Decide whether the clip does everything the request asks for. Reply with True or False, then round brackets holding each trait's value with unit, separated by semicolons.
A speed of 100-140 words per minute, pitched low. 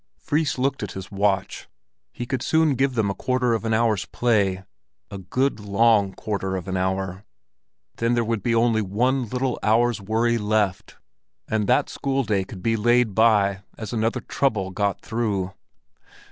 False (170 wpm; 110 Hz)